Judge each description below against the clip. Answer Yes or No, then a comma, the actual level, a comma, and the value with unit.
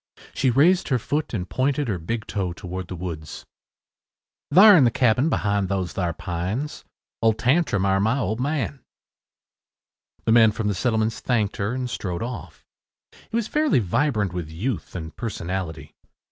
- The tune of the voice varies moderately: No, wide, 5.9 semitones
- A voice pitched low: Yes, low, 110 Hz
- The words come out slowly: No, average, 160 wpm